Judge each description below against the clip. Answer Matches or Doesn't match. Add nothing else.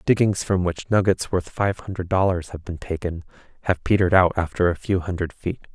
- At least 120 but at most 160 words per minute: Doesn't match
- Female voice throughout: Doesn't match